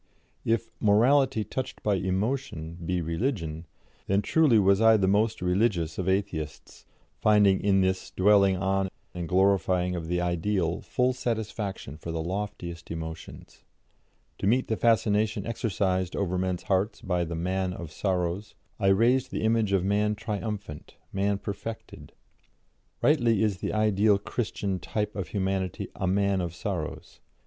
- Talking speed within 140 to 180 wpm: Yes, average, 145 wpm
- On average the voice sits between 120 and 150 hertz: No, very low, 95 Hz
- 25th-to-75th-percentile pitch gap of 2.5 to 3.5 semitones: Yes, average, 3.1 semitones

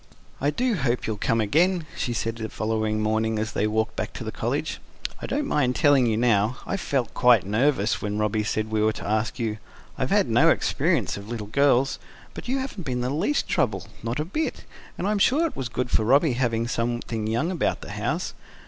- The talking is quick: Yes, fast, 215 wpm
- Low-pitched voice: Yes, low, 120 Hz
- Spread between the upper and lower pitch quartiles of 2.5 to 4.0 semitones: No, average, 4.9 semitones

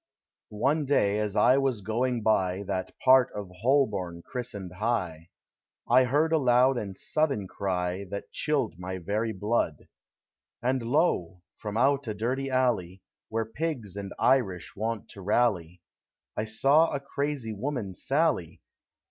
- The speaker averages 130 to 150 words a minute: Yes, average, 140 wpm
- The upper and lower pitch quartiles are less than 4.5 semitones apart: No, wide, 5.5 semitones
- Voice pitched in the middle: No, low, 110 Hz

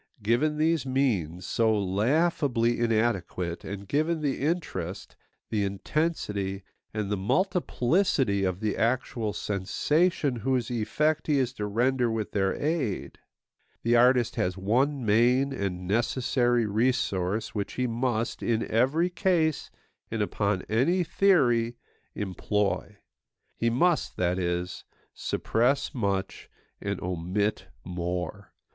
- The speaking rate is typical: No, slow, 115 wpm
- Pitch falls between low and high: No, low, 115 Hz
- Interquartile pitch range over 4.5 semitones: Yes, average, 5.3 semitones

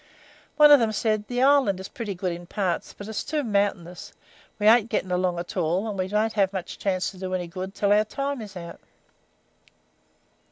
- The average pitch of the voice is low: No, high, 200 Hz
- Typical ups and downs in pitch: Yes, average, 3.1 semitones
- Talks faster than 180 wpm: Yes, fast, 205 wpm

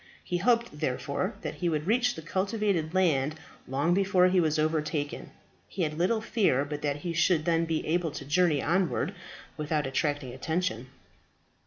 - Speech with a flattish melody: No, average, 3.5 semitones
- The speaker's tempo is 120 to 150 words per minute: No, average, 165 wpm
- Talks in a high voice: No, medium, 165 Hz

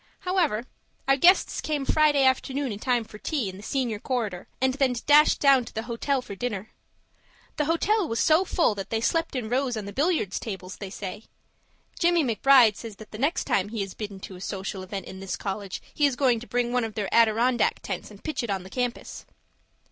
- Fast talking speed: Yes, fast, 215 wpm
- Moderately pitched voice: No, high, 240 Hz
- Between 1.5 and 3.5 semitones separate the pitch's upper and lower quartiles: No, average, 5.2 semitones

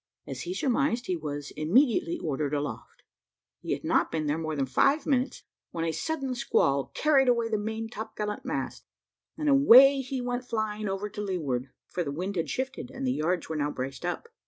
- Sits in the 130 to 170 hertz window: No, high, 210 Hz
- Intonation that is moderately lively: No, wide, 8.6 semitones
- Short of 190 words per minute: No, average, 195 wpm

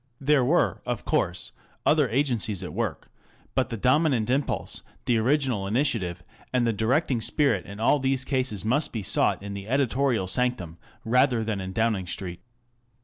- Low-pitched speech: Yes, low, 120 Hz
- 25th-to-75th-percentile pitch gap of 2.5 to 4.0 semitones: No, average, 4.8 semitones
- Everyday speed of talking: Yes, average, 160 wpm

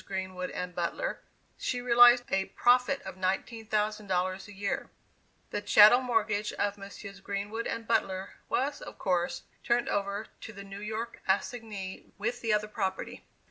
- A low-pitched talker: No, high, 205 Hz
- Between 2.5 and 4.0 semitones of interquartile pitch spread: Yes, average, 3.1 semitones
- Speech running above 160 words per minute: No, average, 145 wpm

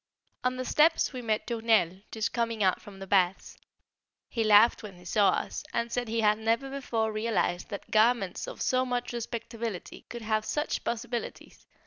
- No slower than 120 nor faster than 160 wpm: No, average, 180 wpm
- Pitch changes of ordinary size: No, narrow, 2.3 semitones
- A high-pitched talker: Yes, high, 225 Hz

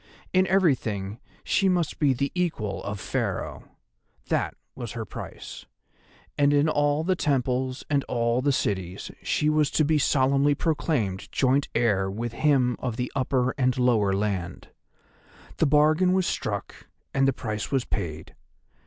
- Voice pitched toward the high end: No, low, 130 Hz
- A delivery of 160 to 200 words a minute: No, average, 145 wpm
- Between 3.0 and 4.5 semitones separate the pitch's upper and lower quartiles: No, average, 5.1 semitones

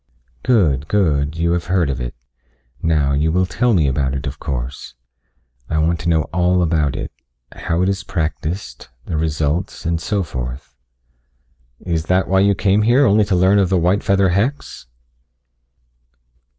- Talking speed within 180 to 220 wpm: No, average, 165 wpm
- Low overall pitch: Yes, very low, 85 Hz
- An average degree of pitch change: Yes, average, 4.4 semitones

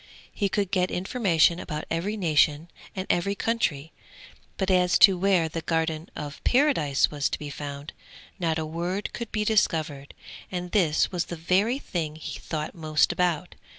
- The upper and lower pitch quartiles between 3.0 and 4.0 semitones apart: Yes, average, 3.7 semitones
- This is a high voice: No, medium, 170 Hz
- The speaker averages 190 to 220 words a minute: No, average, 165 wpm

